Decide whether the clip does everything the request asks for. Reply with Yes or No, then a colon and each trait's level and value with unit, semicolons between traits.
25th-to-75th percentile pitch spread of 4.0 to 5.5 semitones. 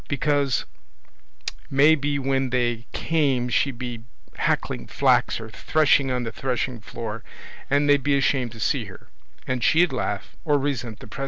No: average, 3.0 semitones